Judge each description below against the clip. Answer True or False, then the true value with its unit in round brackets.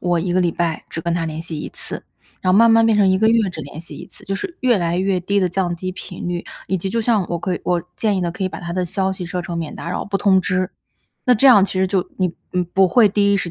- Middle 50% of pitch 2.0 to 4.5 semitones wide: True (2.4 semitones)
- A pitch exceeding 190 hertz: False (185 Hz)